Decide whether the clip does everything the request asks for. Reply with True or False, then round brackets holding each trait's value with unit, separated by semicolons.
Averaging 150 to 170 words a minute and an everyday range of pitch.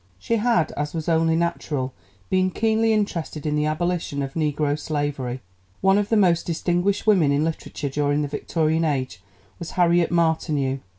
True (165 wpm; 3.3 semitones)